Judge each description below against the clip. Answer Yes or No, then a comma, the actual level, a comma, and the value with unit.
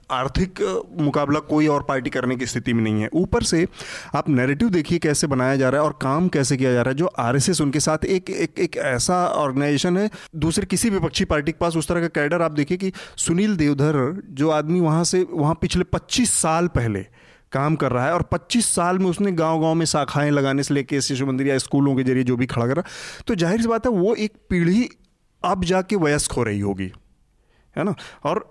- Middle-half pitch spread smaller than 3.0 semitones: No, average, 4.8 semitones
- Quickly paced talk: Yes, fast, 225 wpm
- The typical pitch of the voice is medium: Yes, medium, 155 Hz